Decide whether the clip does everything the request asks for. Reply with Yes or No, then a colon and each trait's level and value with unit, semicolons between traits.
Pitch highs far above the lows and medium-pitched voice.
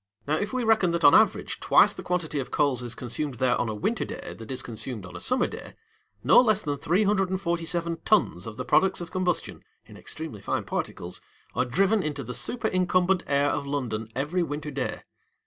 Yes: wide, 6.2 semitones; medium, 155 Hz